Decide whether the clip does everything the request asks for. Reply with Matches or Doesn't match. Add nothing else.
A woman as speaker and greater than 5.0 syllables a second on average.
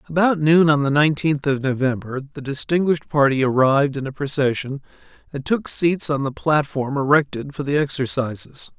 Doesn't match